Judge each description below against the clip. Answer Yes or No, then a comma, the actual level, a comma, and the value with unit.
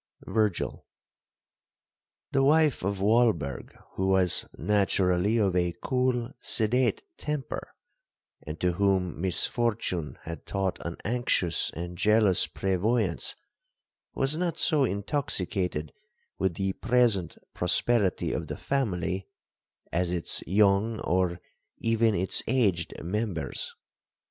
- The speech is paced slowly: Yes, slow, 105 wpm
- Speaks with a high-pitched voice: No, low, 100 Hz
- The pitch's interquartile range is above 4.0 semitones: Yes, average, 4.6 semitones